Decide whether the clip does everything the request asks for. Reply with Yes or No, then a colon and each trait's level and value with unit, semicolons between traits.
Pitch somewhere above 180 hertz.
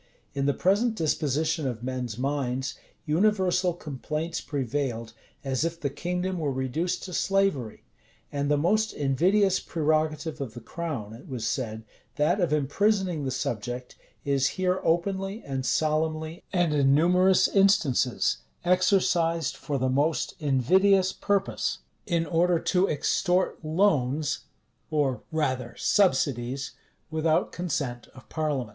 No: medium, 155 Hz